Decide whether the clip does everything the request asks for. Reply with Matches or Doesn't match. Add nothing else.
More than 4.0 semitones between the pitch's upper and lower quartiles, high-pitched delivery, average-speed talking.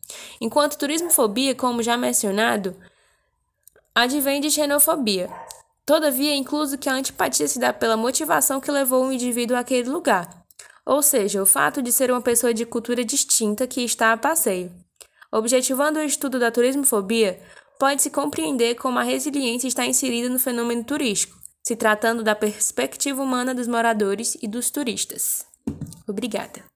Doesn't match